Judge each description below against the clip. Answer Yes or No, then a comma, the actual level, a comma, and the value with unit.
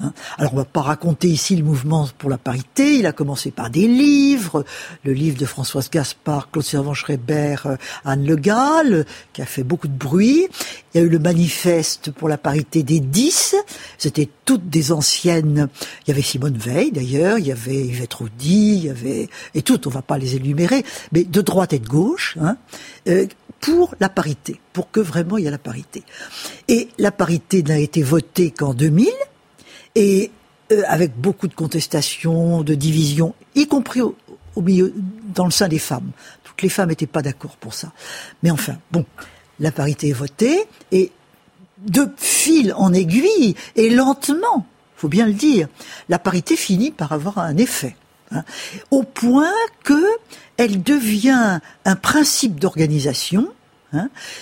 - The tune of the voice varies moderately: No, wide, 6.4 semitones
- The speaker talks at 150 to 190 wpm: Yes, average, 170 wpm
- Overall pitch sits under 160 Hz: No, medium, 170 Hz